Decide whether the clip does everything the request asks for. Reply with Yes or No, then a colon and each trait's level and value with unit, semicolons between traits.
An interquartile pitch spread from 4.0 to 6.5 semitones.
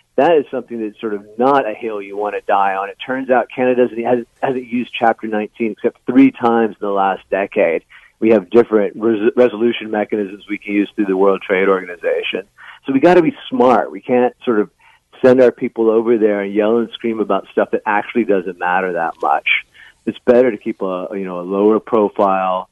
No: average, 3.3 semitones